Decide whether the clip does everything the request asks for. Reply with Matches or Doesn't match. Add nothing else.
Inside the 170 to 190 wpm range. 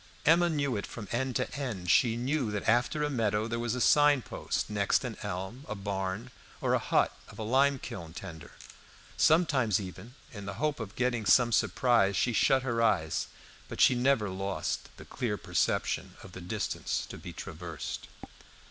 Matches